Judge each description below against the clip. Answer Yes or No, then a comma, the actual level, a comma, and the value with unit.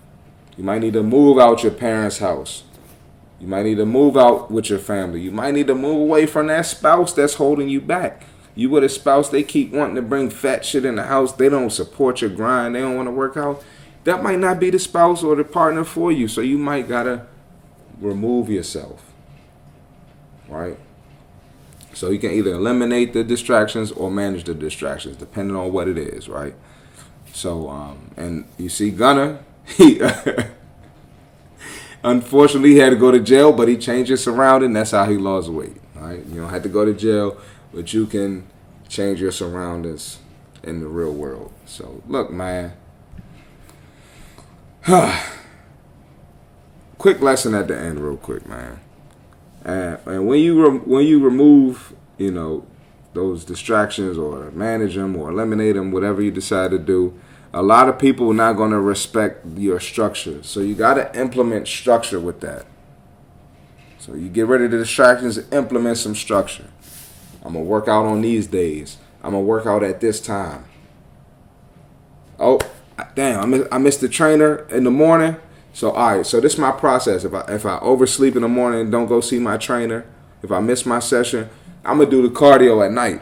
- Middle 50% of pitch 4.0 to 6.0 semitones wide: Yes, wide, 5.5 semitones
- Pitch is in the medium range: No, low, 115 Hz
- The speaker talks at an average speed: Yes, average, 190 wpm